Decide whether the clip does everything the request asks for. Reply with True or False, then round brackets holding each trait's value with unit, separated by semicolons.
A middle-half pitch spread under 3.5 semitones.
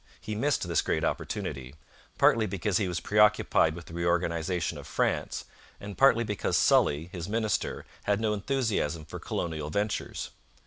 False (4.2 semitones)